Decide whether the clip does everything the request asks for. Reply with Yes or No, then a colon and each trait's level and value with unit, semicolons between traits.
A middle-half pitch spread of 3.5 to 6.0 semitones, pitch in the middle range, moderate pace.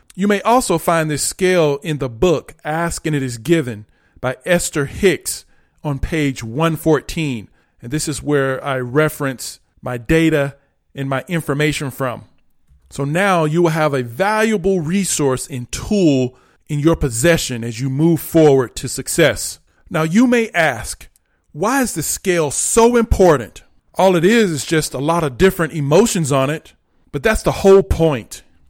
Yes: average, 4.4 semitones; medium, 155 Hz; average, 165 wpm